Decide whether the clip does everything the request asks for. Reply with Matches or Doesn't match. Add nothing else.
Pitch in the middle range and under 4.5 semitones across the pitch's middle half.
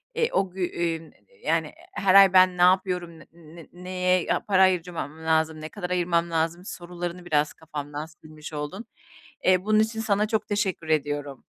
Matches